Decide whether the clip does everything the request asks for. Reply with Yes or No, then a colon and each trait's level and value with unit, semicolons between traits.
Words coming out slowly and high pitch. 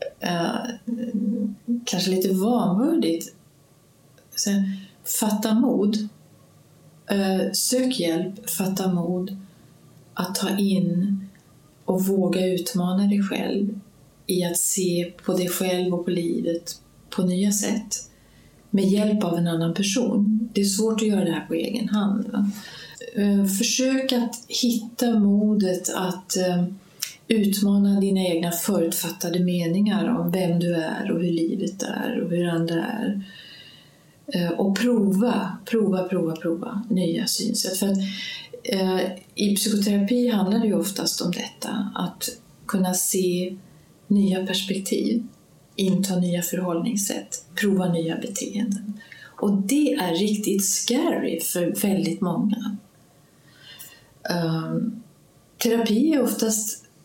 Yes: slow, 115 wpm; high, 195 Hz